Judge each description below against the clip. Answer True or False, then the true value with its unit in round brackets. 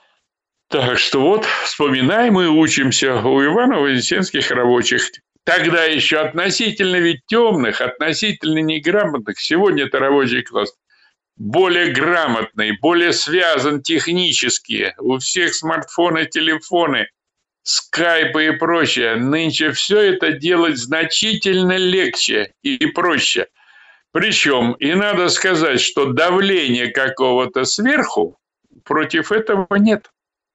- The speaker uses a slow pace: True (100 wpm)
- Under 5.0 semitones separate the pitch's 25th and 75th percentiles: False (5.3 semitones)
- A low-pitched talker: False (160 Hz)